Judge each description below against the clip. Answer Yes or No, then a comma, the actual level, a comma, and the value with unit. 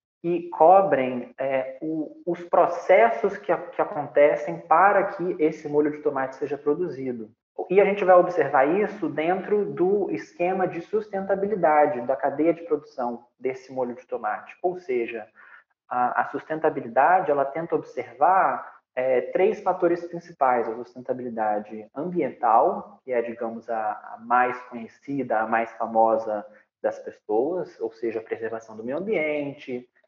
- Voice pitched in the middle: Yes, medium, 155 Hz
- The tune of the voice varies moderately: No, wide, 6.7 semitones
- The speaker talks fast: No, average, 140 wpm